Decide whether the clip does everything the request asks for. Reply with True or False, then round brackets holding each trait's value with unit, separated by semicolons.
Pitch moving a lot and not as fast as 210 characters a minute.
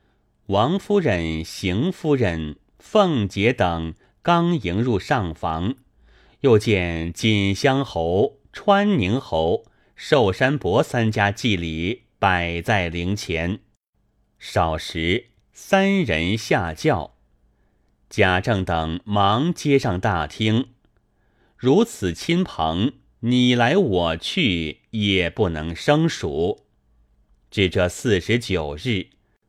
True (6.1 semitones; 135 characters per minute)